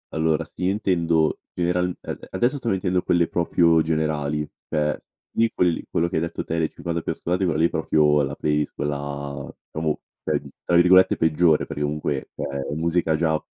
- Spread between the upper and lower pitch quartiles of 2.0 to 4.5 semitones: Yes, narrow, 2.6 semitones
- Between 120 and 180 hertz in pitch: No, very low, 80 Hz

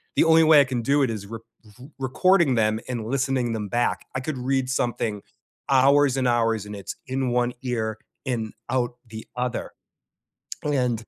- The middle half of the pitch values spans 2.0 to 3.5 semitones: Yes, average, 2.9 semitones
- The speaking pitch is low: Yes, low, 125 Hz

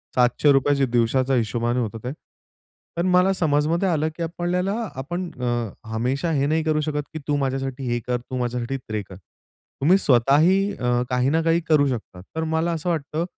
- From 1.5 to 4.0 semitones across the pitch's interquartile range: No, average, 4.9 semitones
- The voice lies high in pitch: No, medium, 140 Hz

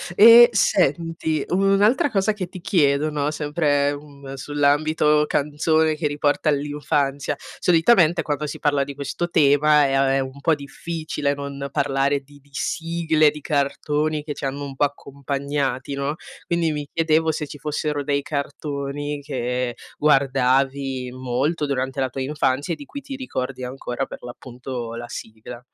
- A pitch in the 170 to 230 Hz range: No, medium, 145 Hz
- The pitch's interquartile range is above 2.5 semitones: No, narrow, 2.2 semitones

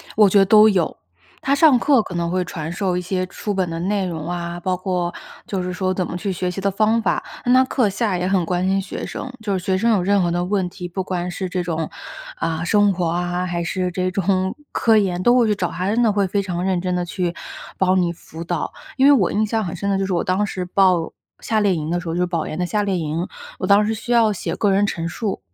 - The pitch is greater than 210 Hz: No, medium, 185 Hz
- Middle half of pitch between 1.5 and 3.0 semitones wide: Yes, narrow, 2.6 semitones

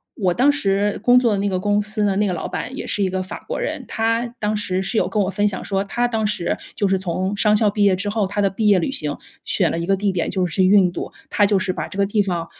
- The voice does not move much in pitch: Yes, narrow, 2.0 semitones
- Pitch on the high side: Yes, high, 200 Hz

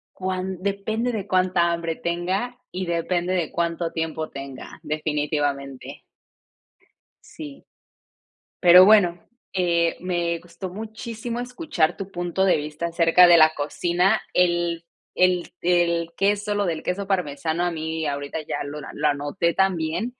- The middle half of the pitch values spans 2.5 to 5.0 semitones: Yes, average, 2.9 semitones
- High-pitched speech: No, medium, 175 Hz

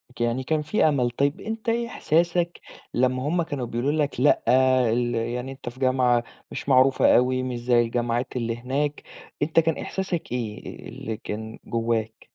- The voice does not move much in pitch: No, average, 3.9 semitones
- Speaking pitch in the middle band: No, low, 130 Hz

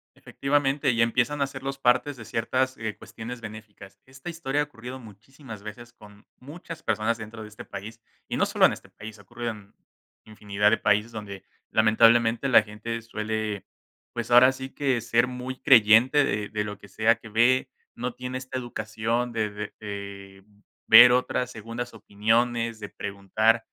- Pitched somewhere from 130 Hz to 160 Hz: No, low, 115 Hz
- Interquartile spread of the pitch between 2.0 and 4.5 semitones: Yes, average, 2.9 semitones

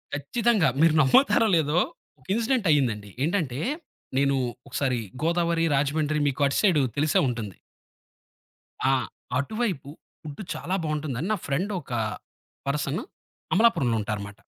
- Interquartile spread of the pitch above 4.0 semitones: Yes, average, 4.6 semitones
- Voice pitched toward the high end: No, medium, 150 Hz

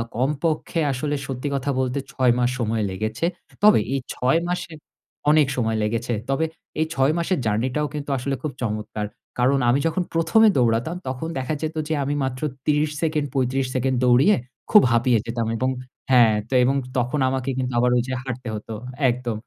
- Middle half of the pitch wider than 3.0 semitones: Yes, average, 3.6 semitones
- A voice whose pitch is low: Yes, low, 130 Hz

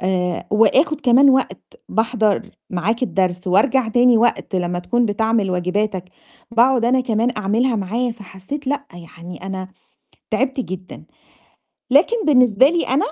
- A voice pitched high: Yes, high, 225 Hz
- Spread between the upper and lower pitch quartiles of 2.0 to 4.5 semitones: No, average, 5.2 semitones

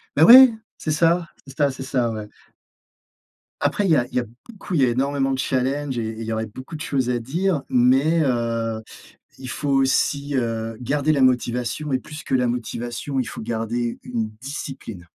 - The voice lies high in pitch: No, low, 130 Hz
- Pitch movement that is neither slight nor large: Yes, average, 3.6 semitones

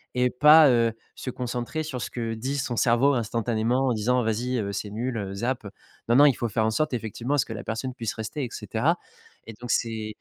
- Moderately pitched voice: No, low, 120 Hz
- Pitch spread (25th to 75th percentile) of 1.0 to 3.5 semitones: Yes, narrow, 2.5 semitones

